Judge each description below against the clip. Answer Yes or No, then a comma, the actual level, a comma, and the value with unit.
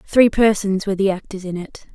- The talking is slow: No, fast, 215 wpm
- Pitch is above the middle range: Yes, high, 200 Hz